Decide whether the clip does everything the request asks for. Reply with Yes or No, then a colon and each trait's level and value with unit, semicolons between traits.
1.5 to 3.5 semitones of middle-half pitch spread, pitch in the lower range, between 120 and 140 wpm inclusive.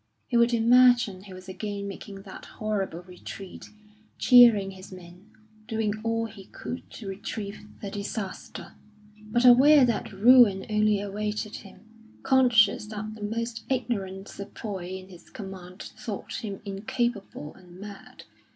No: average, 2.9 semitones; high, 205 Hz; slow, 135 wpm